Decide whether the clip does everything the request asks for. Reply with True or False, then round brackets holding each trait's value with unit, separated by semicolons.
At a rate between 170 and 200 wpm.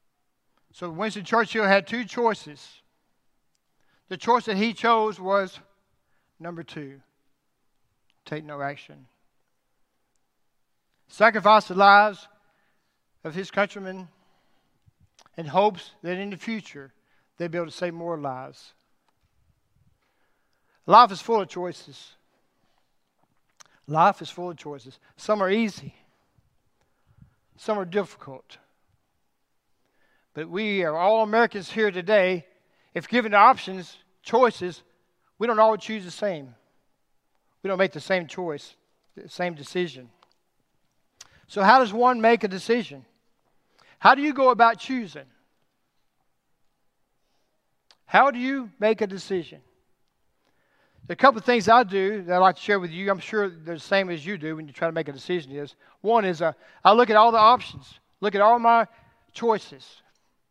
False (140 wpm)